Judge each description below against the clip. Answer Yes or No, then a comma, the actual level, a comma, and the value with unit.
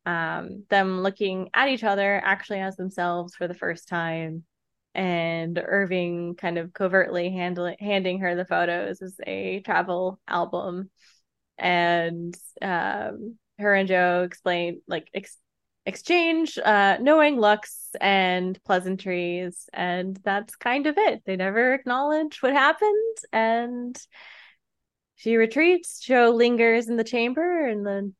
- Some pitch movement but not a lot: Yes, average, 4.7 semitones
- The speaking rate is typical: No, slow, 130 wpm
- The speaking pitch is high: Yes, high, 195 Hz